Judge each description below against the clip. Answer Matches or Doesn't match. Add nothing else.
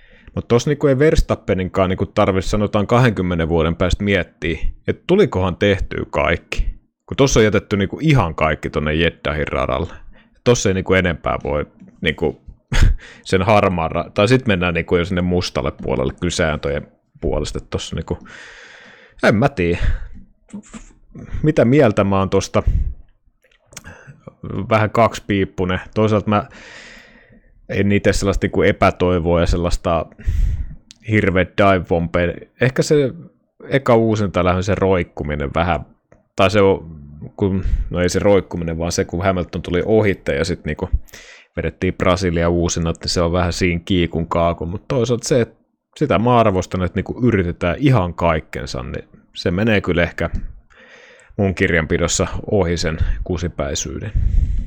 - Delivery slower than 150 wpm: Matches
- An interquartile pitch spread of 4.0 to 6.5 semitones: Doesn't match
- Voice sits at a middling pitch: Doesn't match